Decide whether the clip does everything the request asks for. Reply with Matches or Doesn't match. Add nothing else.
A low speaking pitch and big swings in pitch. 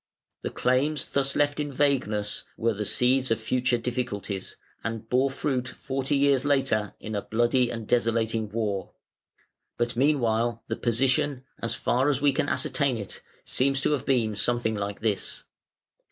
Doesn't match